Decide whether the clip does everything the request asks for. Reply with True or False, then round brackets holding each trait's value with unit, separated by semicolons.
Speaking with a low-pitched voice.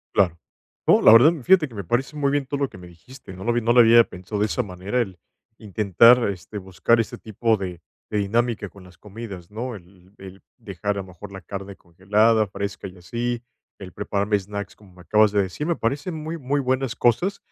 True (105 Hz)